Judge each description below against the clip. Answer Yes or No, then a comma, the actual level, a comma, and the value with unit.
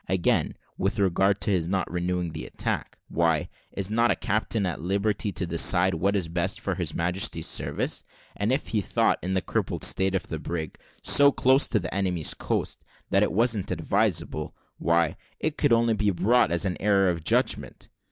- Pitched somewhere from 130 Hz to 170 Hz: No, very low, 95 Hz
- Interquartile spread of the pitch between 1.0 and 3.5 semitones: Yes, average, 3.2 semitones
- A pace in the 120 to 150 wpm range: No, average, 195 wpm